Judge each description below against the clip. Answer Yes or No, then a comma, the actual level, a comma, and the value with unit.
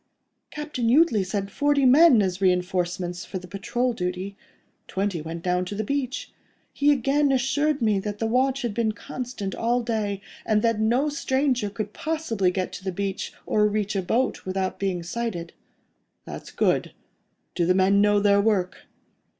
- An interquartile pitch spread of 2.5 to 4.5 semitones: No, average, 4.9 semitones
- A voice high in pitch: Yes, high, 210 Hz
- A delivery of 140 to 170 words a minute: Yes, average, 165 wpm